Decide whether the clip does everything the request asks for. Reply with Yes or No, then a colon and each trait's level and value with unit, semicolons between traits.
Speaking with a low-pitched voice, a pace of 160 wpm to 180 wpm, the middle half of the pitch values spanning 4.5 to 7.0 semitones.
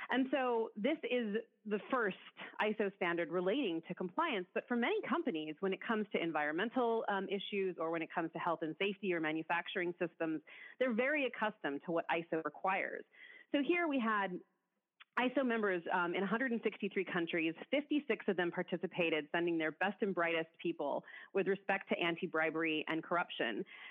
No: high, 195 Hz; average, 170 wpm; average, 5.2 semitones